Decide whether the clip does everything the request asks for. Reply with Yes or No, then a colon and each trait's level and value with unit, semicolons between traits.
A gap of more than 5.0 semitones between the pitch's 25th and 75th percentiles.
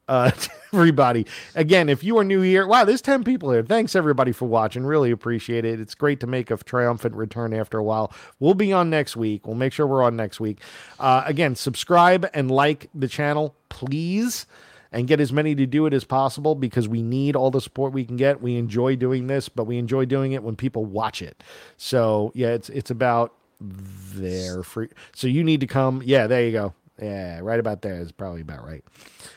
No: average, 4.7 semitones